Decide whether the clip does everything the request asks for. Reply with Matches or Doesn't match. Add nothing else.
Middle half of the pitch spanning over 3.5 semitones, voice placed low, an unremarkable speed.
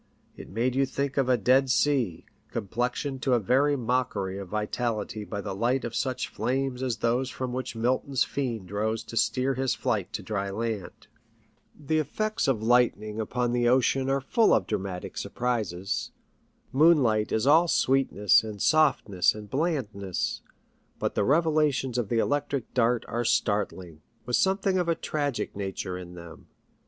Matches